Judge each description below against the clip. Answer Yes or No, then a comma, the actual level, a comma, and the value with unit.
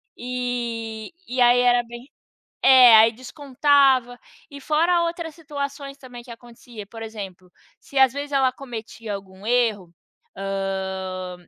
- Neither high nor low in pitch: No, high, 245 Hz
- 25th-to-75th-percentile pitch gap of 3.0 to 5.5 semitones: Yes, average, 3.9 semitones